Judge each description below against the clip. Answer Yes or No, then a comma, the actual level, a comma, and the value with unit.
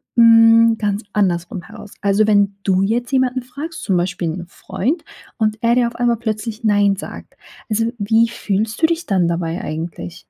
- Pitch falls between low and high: No, high, 215 Hz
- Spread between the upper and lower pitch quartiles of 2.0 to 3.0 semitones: No, average, 3.4 semitones